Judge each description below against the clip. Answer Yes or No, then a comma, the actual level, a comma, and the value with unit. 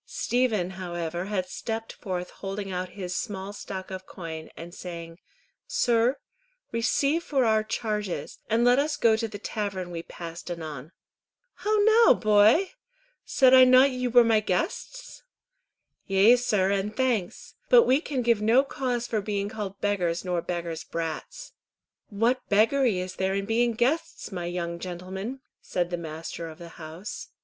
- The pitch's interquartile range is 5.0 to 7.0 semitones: Yes, average, 5.3 semitones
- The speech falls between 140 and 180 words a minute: Yes, average, 155 wpm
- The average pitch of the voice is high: Yes, high, 205 Hz